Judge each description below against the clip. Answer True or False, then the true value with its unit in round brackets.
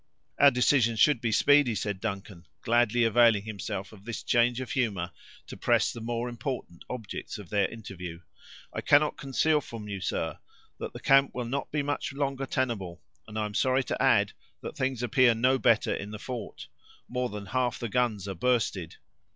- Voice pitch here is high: False (115 Hz)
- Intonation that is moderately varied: True (3.7 semitones)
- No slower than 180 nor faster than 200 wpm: True (185 wpm)